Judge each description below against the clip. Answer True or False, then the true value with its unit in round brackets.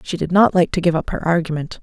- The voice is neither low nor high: True (170 Hz)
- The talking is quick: True (295 wpm)